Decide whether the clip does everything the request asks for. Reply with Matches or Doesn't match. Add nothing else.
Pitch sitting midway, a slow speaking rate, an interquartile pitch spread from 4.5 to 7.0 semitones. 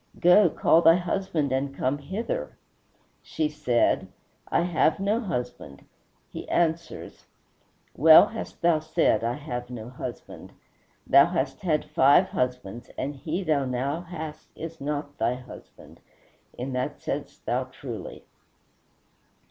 Matches